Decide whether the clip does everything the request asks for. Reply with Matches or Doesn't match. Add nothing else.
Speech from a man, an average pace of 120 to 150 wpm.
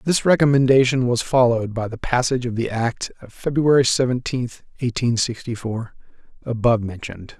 Matches